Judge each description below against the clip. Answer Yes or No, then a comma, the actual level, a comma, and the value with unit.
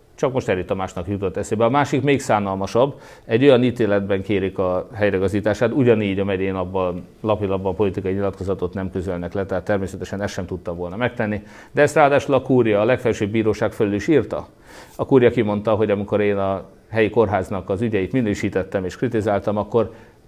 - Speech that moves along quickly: Yes, fast, 175 wpm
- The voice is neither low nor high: No, low, 105 Hz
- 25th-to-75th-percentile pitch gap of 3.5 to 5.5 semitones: No, average, 2.7 semitones